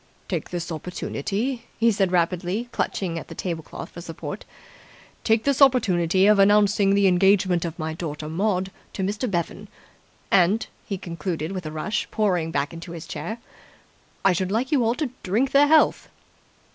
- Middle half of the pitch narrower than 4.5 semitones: Yes, average, 4.0 semitones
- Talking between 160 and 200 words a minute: Yes, average, 170 wpm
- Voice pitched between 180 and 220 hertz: Yes, high, 190 Hz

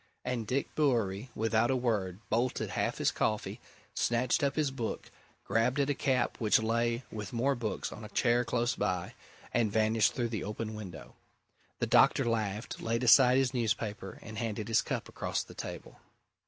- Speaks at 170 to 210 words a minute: Yes, average, 175 wpm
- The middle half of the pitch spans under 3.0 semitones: Yes, narrow, 2.5 semitones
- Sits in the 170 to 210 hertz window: No, low, 115 Hz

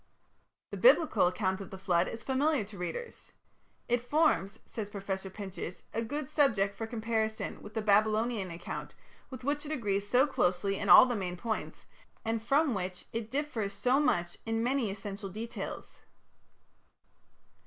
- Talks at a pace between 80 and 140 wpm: No, average, 155 wpm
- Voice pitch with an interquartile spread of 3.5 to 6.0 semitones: Yes, average, 4.4 semitones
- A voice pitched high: Yes, high, 220 Hz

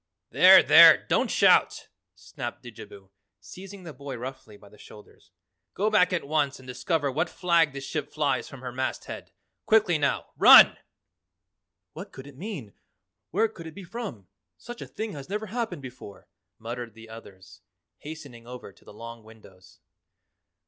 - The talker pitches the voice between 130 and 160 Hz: Yes, medium, 140 Hz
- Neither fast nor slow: Yes, average, 160 wpm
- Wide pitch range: Yes, wide, 7.4 semitones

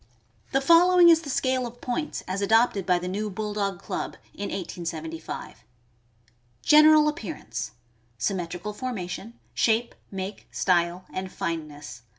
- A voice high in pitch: Yes, high, 200 Hz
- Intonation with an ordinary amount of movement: No, wide, 6.0 semitones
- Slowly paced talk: Yes, slow, 130 wpm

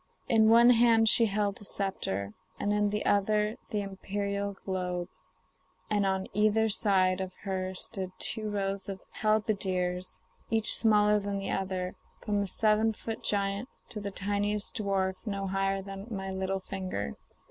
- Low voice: No, high, 200 Hz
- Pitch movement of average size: No, narrow, 1.8 semitones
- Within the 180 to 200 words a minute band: No, average, 160 wpm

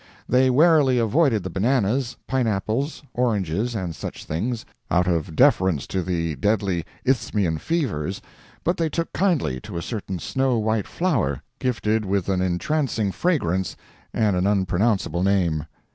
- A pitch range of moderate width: No, wide, 6.0 semitones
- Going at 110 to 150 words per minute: Yes, average, 140 wpm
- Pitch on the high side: No, low, 105 Hz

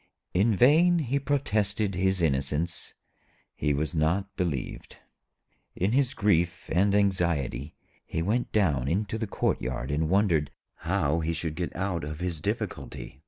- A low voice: Yes, very low, 90 Hz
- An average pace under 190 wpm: Yes, average, 140 wpm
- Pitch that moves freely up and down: No, average, 4.8 semitones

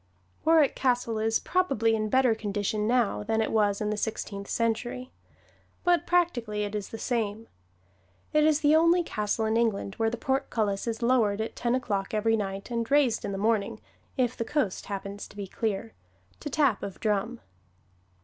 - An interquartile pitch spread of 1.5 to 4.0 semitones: Yes, average, 3.3 semitones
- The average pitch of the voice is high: Yes, high, 225 Hz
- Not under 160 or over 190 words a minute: Yes, average, 180 wpm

